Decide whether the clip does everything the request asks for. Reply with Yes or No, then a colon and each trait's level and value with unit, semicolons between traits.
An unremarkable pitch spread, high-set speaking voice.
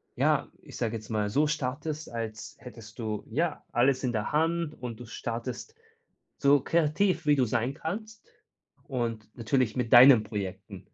No: average, 5.0 semitones; low, 125 Hz